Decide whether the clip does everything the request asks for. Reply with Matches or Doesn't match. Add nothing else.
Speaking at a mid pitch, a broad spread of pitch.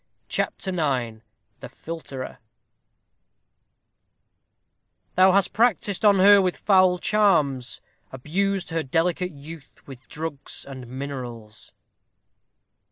Matches